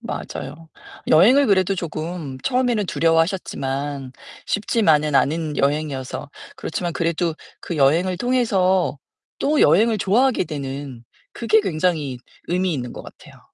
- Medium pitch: Yes, medium, 165 Hz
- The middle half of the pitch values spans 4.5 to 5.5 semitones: Yes, average, 5.1 semitones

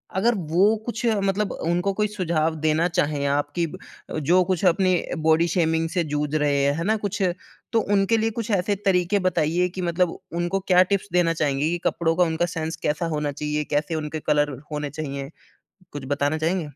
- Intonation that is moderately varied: Yes, average, 3.4 semitones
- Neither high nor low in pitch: Yes, medium, 170 Hz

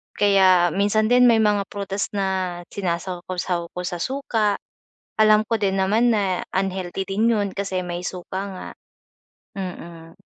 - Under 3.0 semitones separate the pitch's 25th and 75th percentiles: Yes, narrow, 2.4 semitones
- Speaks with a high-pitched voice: Yes, high, 195 Hz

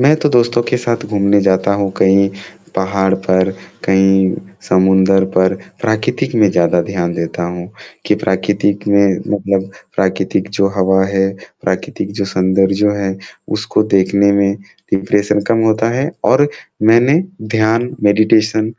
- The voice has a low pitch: Yes, low, 100 Hz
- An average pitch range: No, narrow, 2.2 semitones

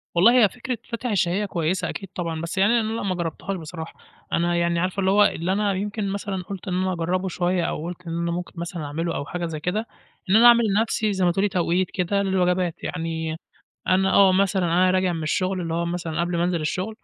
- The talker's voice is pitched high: No, medium, 180 Hz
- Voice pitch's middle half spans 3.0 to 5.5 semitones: No, narrow, 2.5 semitones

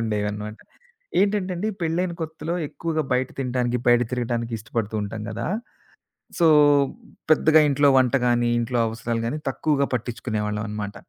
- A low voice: Yes, low, 120 Hz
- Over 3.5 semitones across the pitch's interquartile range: Yes, wide, 5.5 semitones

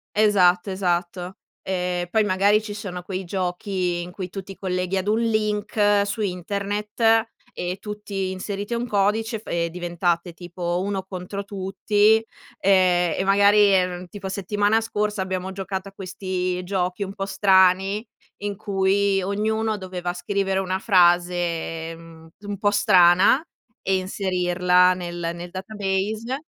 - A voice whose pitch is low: No, high, 190 Hz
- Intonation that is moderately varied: No, narrow, 2.3 semitones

